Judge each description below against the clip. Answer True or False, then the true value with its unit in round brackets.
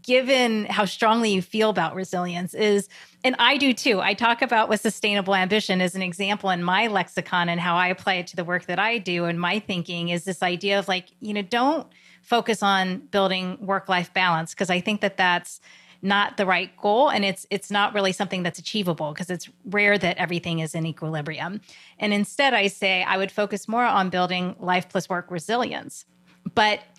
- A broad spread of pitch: False (2.7 semitones)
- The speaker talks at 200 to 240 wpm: True (205 wpm)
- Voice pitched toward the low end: False (190 Hz)